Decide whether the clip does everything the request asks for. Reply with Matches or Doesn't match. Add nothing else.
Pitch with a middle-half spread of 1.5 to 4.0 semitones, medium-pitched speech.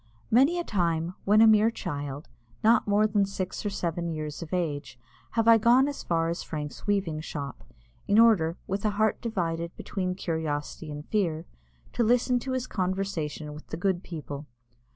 Doesn't match